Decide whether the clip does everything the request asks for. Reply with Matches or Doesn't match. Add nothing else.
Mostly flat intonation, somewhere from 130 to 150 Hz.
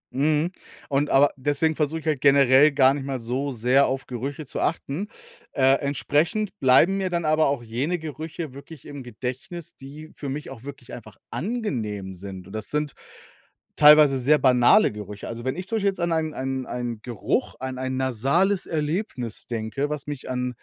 Doesn't match